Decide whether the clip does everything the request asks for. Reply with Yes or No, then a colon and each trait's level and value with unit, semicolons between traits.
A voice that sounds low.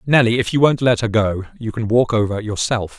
Yes: low, 115 Hz